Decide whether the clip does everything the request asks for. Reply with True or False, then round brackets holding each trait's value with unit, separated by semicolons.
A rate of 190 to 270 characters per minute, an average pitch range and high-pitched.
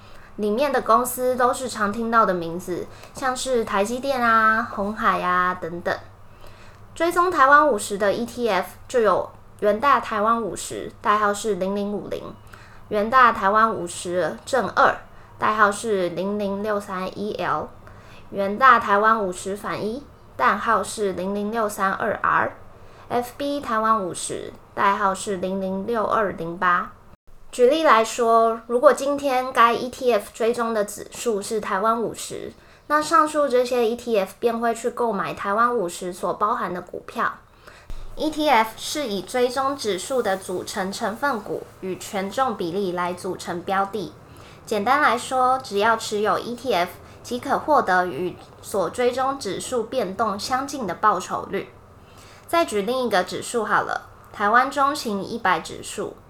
True (225 characters per minute; 4.4 semitones; 220 Hz)